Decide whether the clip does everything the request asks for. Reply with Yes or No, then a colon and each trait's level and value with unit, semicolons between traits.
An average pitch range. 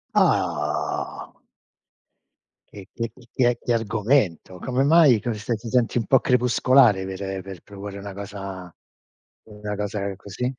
Yes: average, 3.8 semitones